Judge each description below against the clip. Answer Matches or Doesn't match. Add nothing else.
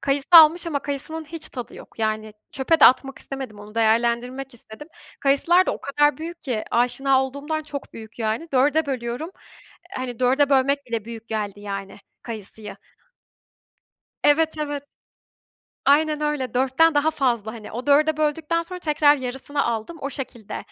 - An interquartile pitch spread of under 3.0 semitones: Doesn't match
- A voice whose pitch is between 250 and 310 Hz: Matches